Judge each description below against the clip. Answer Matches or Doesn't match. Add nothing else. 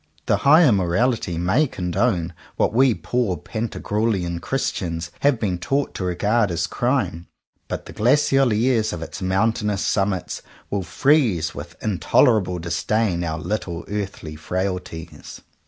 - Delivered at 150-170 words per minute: Doesn't match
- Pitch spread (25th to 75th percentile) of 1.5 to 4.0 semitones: Doesn't match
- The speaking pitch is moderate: Doesn't match